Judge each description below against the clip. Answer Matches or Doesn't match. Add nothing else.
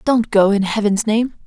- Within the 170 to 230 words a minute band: Matches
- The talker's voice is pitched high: Matches